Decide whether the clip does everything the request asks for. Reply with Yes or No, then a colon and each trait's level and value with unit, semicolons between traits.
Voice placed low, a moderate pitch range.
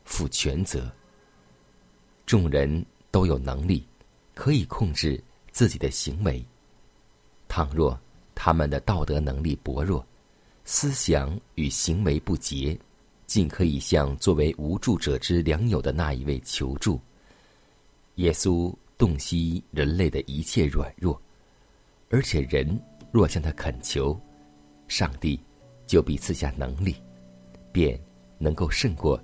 Yes: very low, 75 Hz; average, 4.2 semitones